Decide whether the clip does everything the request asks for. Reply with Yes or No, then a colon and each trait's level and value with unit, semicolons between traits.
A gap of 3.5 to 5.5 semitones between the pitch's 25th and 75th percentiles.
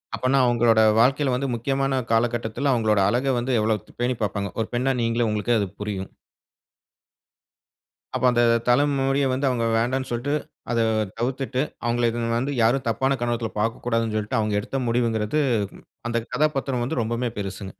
No: average, 2.8 semitones